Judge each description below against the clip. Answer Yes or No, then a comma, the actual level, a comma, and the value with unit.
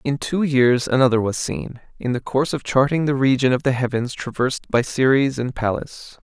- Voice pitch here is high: No, low, 130 Hz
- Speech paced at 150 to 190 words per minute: No, average, 200 wpm